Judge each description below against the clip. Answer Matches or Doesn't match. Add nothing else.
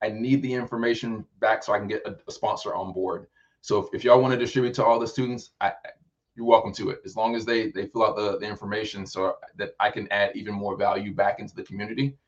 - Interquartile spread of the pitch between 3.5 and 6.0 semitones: Doesn't match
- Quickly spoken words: Matches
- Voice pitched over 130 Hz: Doesn't match